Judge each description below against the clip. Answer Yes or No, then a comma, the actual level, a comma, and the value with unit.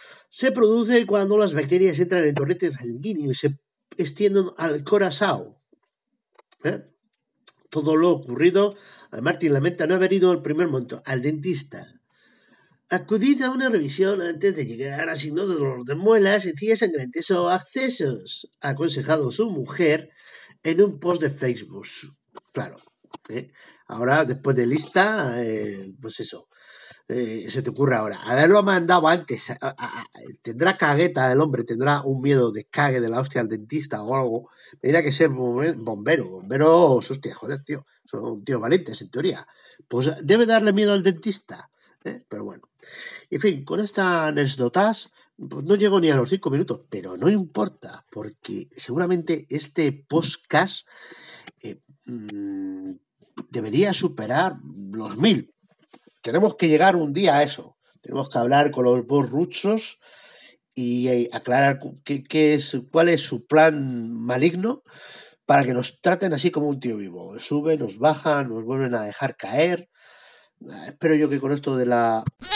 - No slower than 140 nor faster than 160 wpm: Yes, average, 155 wpm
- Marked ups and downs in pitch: Yes, wide, 6.2 semitones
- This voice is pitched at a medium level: Yes, medium, 155 Hz